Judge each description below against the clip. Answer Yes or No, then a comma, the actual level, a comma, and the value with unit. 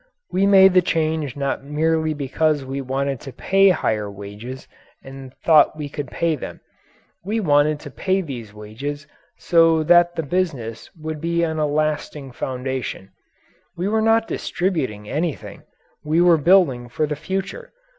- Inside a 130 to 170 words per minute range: Yes, average, 155 wpm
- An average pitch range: Yes, average, 4.3 semitones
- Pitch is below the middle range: No, medium, 150 Hz